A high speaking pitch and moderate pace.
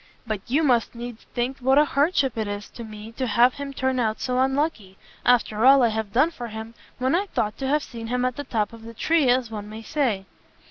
No: high, 245 Hz; fast, 240 wpm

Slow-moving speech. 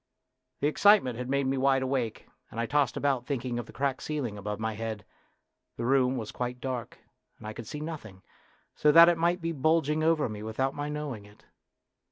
No: fast, 205 wpm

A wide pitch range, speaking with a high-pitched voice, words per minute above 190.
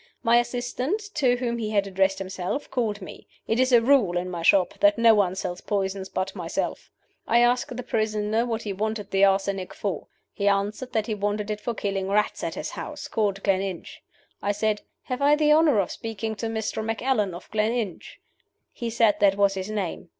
No: average, 3.2 semitones; high, 210 Hz; average, 200 wpm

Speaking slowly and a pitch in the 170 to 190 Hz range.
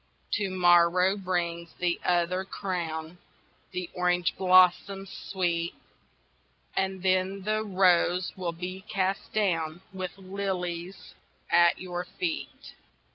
Yes: slow, 105 wpm; medium, 185 Hz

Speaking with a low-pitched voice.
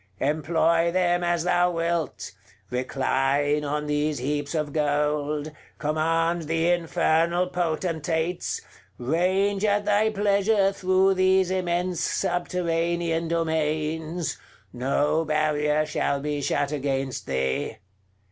No: medium, 165 Hz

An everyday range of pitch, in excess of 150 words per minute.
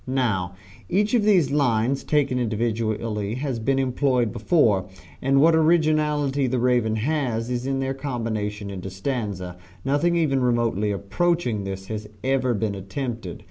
No: average, 4.6 semitones; average, 140 wpm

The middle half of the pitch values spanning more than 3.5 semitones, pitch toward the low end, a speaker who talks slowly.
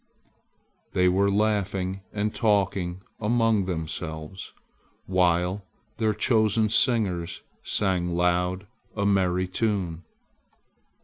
No: average, 2.9 semitones; very low, 95 Hz; slow, 85 wpm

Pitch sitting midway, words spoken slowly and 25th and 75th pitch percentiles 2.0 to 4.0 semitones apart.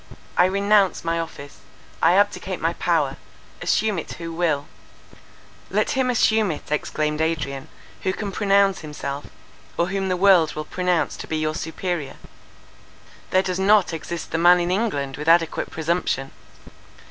No: medium, 175 Hz; average, 145 wpm; average, 3.7 semitones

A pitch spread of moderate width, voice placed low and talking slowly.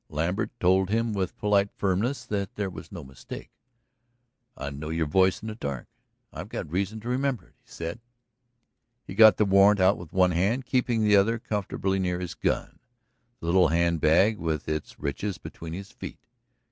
No: average, 4.0 semitones; very low, 95 Hz; average, 185 wpm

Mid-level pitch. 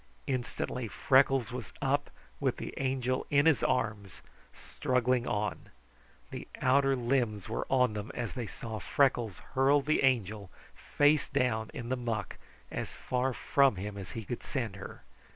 No: low, 125 Hz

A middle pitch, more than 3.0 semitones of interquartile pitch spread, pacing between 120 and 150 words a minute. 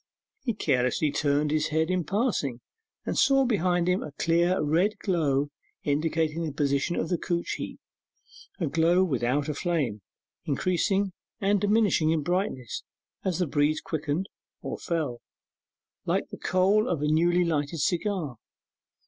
Yes: medium, 165 Hz; average, 3.9 semitones; average, 145 wpm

